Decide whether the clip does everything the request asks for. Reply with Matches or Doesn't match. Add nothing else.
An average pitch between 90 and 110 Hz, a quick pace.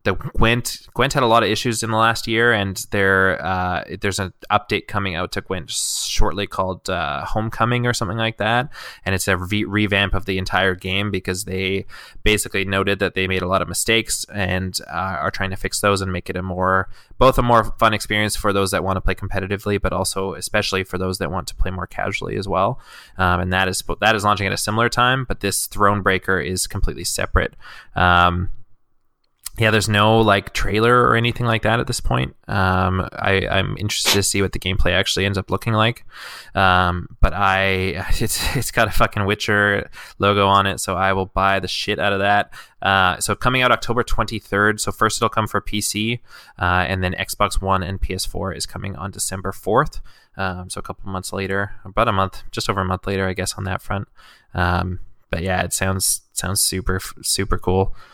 Matches